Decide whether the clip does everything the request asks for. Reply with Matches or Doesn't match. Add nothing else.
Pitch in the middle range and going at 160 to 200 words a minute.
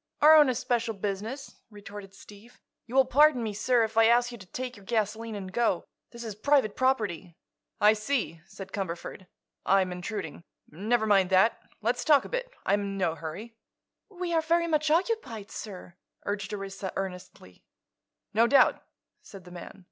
Doesn't match